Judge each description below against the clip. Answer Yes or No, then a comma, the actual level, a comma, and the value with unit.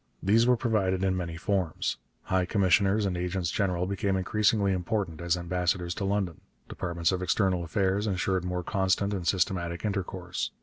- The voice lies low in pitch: Yes, very low, 95 Hz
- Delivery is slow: No, average, 160 wpm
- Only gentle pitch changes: Yes, narrow, 2.0 semitones